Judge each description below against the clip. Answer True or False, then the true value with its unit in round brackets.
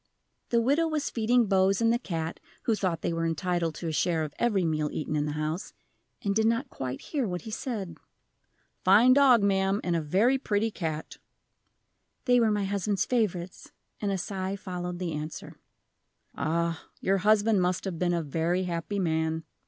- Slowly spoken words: False (185 wpm)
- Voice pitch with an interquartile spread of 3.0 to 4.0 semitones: False (4.7 semitones)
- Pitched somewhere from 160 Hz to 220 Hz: True (190 Hz)